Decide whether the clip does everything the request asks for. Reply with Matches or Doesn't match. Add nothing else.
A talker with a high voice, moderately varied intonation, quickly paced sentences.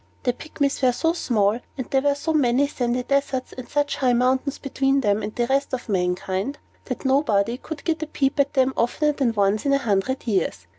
Matches